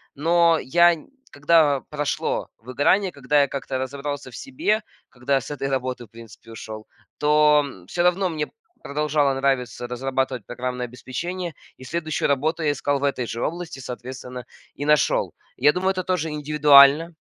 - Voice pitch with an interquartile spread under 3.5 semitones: No, average, 3.8 semitones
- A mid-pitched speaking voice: Yes, medium, 145 Hz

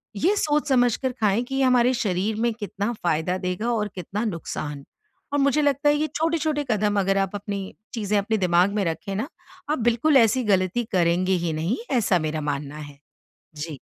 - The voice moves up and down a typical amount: No, wide, 5.9 semitones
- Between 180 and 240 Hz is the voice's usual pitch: Yes, high, 205 Hz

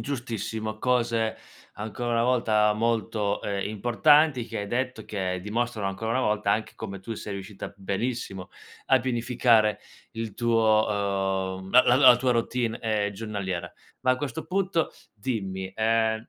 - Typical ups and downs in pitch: Yes, average, 3.0 semitones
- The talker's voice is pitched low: Yes, low, 110 Hz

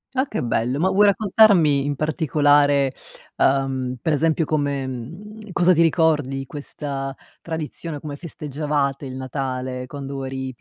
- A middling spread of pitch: Yes, average, 3.1 semitones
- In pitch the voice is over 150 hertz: No, medium, 145 Hz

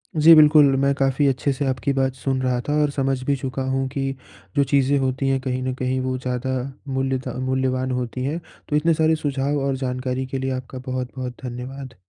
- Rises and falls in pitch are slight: Yes, narrow, 1.3 semitones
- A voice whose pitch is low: Yes, low, 130 Hz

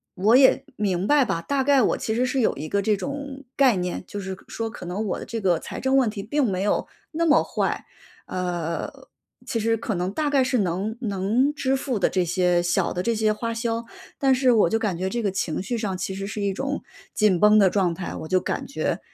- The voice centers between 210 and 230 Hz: Yes, high, 215 Hz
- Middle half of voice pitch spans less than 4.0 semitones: No, average, 5.3 semitones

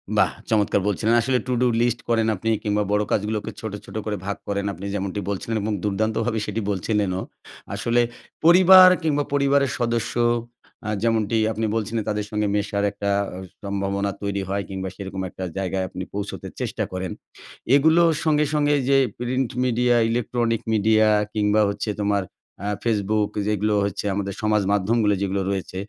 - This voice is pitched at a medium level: No, low, 105 Hz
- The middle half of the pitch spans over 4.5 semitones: No, average, 2.7 semitones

